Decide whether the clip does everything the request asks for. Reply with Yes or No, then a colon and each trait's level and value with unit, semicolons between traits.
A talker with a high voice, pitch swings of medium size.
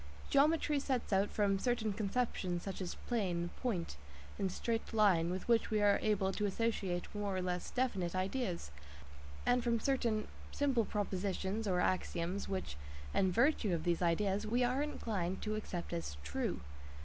Yes: high, 200 Hz; average, 4.2 semitones